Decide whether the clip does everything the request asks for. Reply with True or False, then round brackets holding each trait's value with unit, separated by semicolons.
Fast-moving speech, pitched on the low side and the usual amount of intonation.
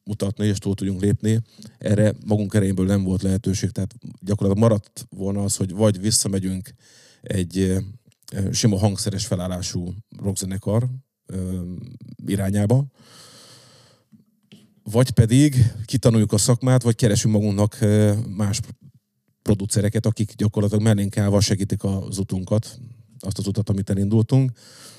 False (115 wpm; 105 Hz; 3.0 semitones)